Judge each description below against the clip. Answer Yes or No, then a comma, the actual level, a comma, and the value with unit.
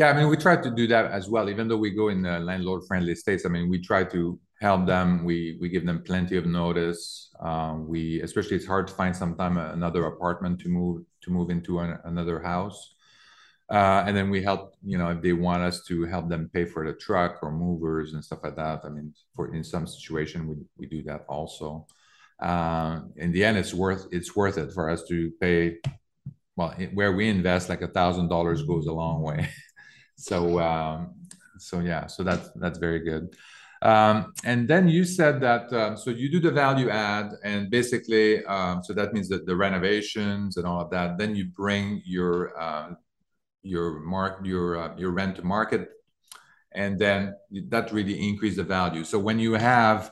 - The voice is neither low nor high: No, very low, 90 Hz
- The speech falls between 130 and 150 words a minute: No, average, 200 wpm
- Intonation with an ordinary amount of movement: Yes, average, 3.2 semitones